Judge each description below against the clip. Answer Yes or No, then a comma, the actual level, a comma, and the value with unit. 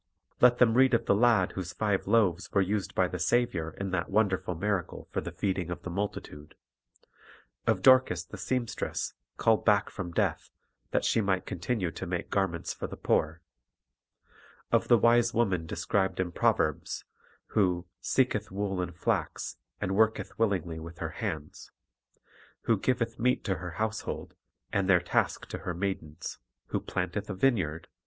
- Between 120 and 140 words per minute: No, average, 170 wpm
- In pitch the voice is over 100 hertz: No, very low, 95 Hz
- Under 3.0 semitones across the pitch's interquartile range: No, average, 4.1 semitones